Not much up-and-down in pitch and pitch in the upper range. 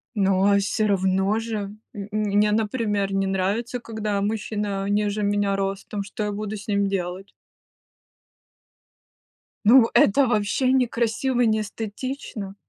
Yes: narrow, 1.9 semitones; high, 205 Hz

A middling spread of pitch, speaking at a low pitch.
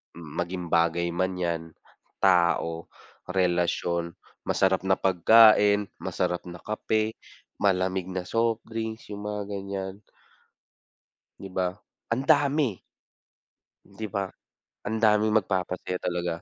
Yes: average, 3.4 semitones; very low, 95 Hz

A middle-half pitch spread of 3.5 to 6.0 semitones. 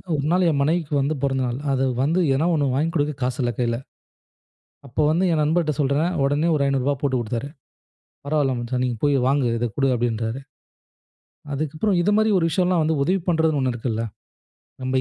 Yes: average, 3.8 semitones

